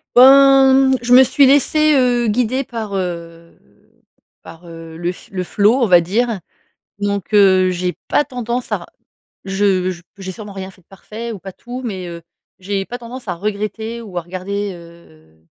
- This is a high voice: Yes, high, 200 Hz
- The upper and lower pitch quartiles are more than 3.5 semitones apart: Yes, average, 5.0 semitones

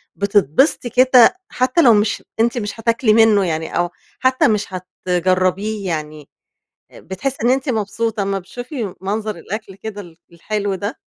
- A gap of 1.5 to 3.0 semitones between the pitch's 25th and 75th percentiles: No, average, 3.8 semitones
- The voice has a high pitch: Yes, high, 205 Hz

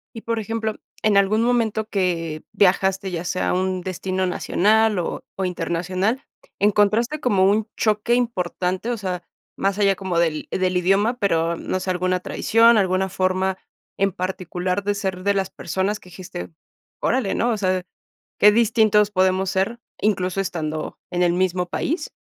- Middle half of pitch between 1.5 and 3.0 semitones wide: Yes, average, 2.7 semitones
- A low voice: No, high, 190 Hz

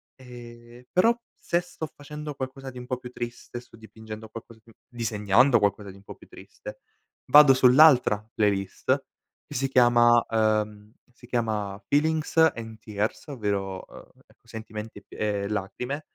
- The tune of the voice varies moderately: Yes, average, 3.6 semitones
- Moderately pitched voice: No, low, 120 Hz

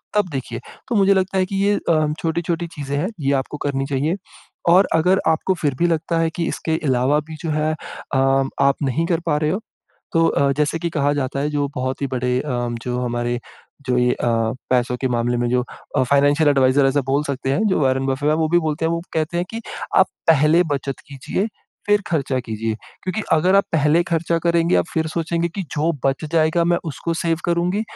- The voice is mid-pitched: Yes, medium, 150 Hz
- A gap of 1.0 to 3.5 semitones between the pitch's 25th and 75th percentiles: No, average, 4.0 semitones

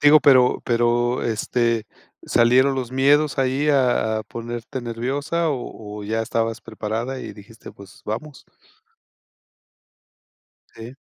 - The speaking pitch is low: Yes, low, 120 Hz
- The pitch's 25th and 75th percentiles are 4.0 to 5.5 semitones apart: No, average, 2.8 semitones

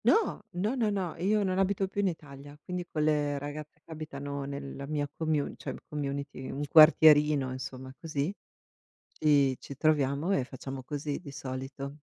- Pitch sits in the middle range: Yes, medium, 145 Hz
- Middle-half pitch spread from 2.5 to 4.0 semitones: Yes, average, 2.8 semitones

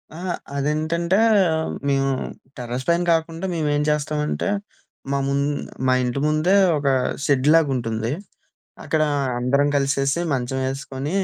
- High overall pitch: No, medium, 140 Hz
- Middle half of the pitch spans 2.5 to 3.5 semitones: Yes, average, 2.8 semitones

